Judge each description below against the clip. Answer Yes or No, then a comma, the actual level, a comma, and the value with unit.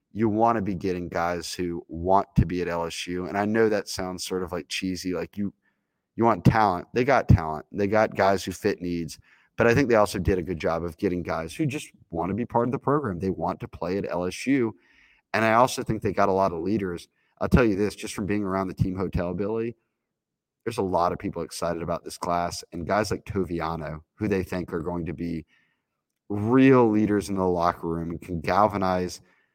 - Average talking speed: No, fast, 230 wpm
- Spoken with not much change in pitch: No, average, 3.6 semitones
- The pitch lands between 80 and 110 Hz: Yes, very low, 95 Hz